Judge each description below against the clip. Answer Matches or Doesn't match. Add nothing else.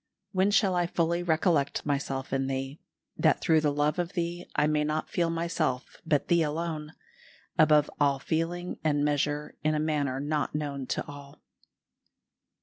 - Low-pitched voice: Doesn't match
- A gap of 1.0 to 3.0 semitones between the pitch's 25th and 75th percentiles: Matches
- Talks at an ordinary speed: Matches